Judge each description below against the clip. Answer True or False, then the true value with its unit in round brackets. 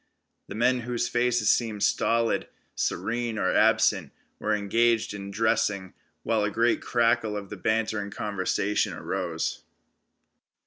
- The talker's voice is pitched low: True (110 Hz)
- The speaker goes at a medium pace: False (120 wpm)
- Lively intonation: False (2.4 semitones)